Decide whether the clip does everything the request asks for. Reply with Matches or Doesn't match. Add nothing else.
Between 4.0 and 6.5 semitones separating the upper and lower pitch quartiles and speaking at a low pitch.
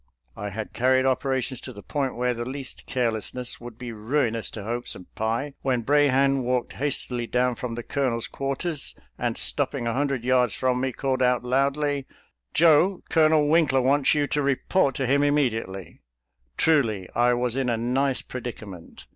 Doesn't match